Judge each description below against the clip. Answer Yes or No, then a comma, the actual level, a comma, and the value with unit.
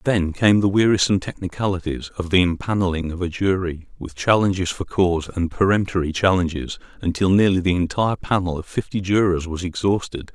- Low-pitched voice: Yes, very low, 90 Hz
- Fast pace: No, average, 160 wpm